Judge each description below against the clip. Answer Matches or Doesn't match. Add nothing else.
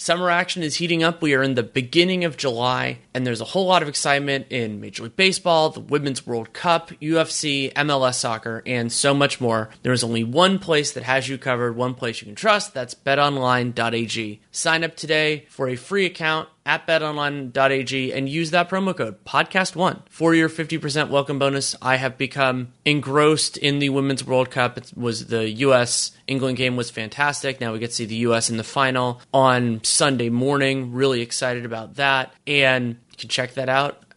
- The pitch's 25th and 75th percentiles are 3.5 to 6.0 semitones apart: Matches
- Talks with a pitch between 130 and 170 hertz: Matches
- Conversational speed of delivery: Matches